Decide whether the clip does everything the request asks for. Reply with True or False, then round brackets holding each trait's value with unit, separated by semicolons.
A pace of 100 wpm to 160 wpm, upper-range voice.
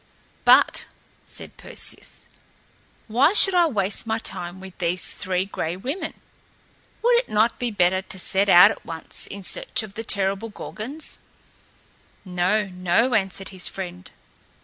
True (145 wpm; 195 Hz)